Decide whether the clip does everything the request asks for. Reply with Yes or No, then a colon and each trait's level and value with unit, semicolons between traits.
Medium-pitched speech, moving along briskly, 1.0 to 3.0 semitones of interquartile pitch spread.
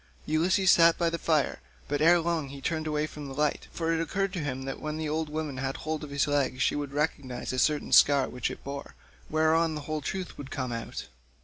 Yes: medium, 150 Hz; fast, 235 wpm; narrow, 2.6 semitones